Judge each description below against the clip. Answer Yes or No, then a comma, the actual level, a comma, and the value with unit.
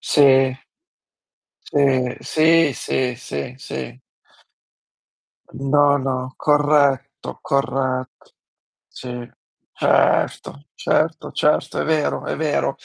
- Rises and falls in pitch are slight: Yes, narrow, 2.3 semitones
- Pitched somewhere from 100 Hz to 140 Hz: Yes, low, 135 Hz